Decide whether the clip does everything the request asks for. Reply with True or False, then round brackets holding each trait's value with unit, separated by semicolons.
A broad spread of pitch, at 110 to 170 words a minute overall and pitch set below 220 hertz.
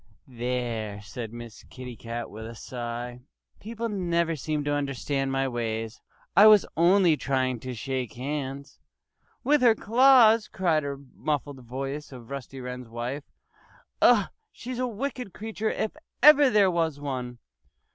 True (7.8 semitones; 145 wpm; 140 Hz)